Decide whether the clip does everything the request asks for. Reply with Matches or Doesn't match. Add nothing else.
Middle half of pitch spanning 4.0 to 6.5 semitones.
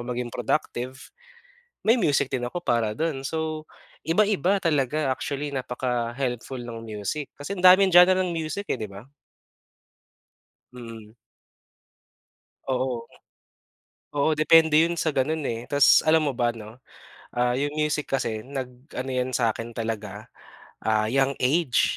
Matches